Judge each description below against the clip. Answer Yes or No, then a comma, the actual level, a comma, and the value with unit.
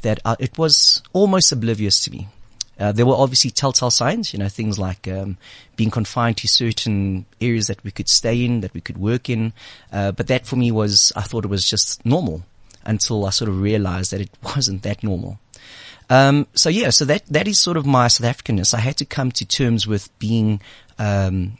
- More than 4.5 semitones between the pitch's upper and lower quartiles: No, average, 3.9 semitones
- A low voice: Yes, low, 115 Hz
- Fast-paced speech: Yes, fast, 210 wpm